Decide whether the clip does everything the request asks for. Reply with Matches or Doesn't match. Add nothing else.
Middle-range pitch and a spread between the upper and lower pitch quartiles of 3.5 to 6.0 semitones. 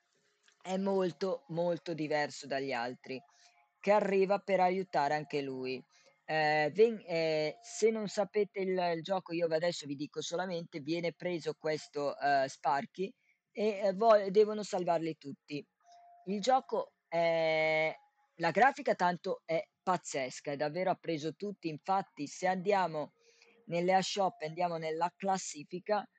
Matches